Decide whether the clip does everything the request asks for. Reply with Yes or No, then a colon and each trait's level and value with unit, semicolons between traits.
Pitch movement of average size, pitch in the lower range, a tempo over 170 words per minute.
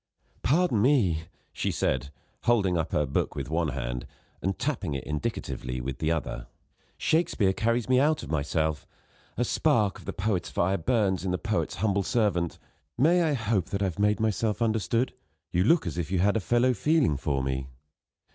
No: wide, 6.6 semitones; very low, 95 Hz; average, 185 wpm